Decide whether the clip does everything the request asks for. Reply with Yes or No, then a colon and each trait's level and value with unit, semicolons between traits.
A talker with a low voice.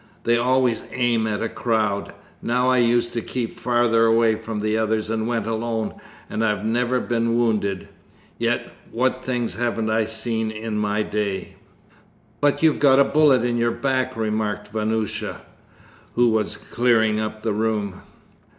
Yes: low, 115 Hz